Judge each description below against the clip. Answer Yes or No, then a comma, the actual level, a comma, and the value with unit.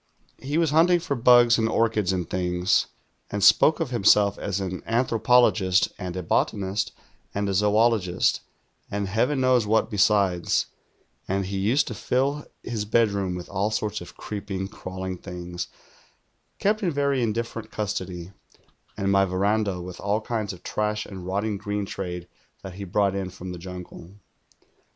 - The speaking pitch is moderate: No, low, 100 Hz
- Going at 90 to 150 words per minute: No, average, 160 wpm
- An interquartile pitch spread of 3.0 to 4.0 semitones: Yes, average, 3.4 semitones